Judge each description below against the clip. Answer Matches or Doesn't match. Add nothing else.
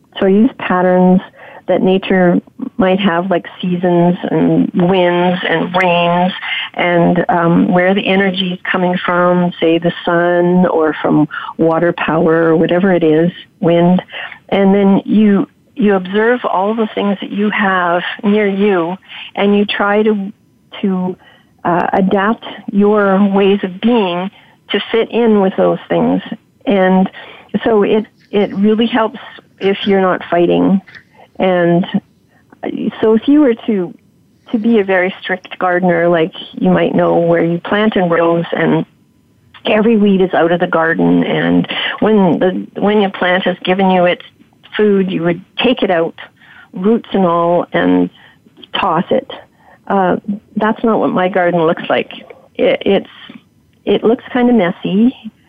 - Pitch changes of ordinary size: Matches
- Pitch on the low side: Doesn't match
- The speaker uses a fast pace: Doesn't match